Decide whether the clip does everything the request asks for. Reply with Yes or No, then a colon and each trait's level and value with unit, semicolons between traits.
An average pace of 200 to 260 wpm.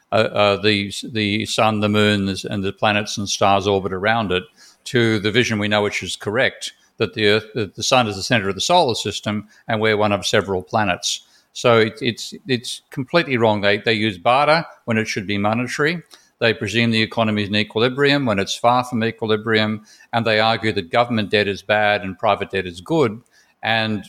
Yes: fast, 205 wpm